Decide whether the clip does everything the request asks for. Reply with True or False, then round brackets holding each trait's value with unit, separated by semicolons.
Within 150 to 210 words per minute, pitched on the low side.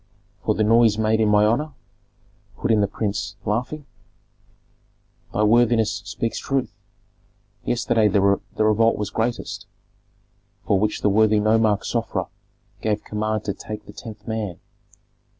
False (135 wpm; 110 Hz)